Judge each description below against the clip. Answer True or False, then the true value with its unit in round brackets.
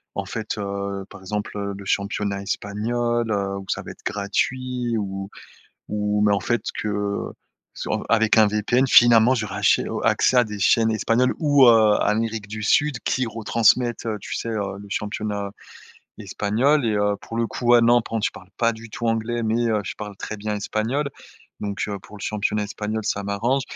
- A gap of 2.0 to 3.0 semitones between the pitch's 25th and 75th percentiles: True (2.4 semitones)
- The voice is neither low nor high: False (110 Hz)